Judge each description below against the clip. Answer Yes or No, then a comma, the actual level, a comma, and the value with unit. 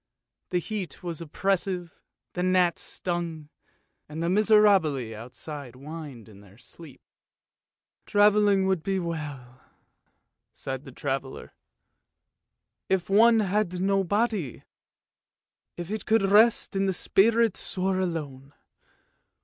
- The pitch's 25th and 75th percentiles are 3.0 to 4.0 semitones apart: No, average, 5.3 semitones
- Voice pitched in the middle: Yes, medium, 175 Hz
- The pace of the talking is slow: Yes, slow, 120 wpm